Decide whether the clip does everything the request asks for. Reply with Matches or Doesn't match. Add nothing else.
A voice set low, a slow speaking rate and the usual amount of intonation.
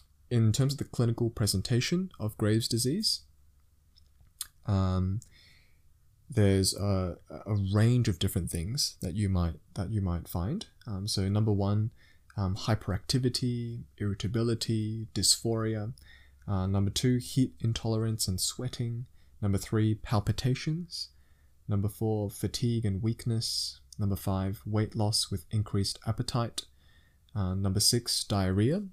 Matches